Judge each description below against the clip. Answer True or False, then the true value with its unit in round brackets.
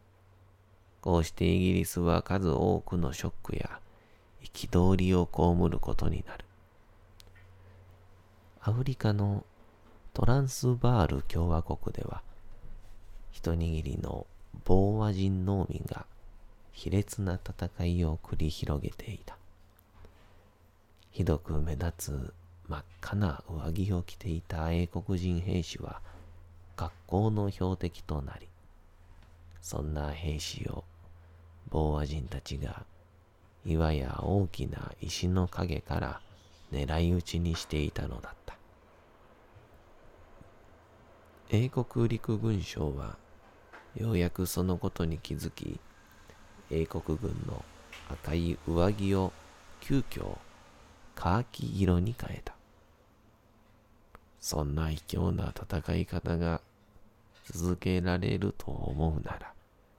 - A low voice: True (90 Hz)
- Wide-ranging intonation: False (3.1 semitones)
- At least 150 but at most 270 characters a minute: True (195 characters per minute)